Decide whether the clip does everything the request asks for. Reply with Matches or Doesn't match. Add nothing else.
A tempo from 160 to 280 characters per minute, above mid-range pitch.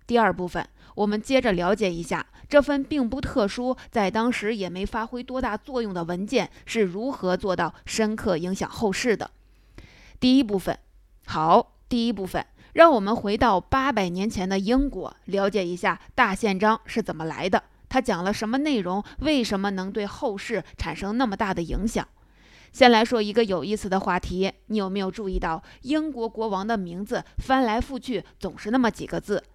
Matches